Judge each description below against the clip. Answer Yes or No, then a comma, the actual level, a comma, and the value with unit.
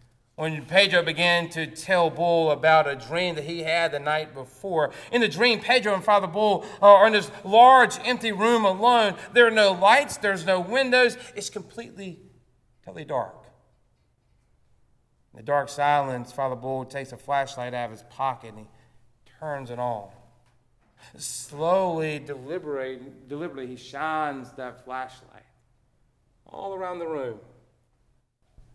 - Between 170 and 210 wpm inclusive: No, average, 145 wpm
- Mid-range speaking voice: Yes, medium, 150 Hz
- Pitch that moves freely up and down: Yes, wide, 7.7 semitones